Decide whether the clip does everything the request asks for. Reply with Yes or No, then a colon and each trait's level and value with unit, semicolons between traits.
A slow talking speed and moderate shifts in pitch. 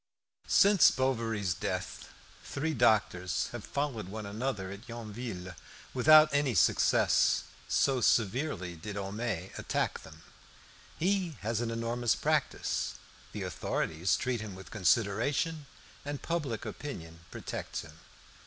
No: slow, 115 wpm; wide, 5.7 semitones